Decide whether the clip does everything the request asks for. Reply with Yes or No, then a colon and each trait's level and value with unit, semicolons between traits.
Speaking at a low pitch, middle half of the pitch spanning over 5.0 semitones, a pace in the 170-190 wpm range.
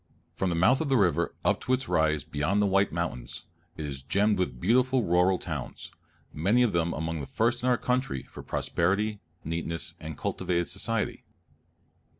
Yes: very low, 90 Hz; wide, 5.6 semitones; average, 175 wpm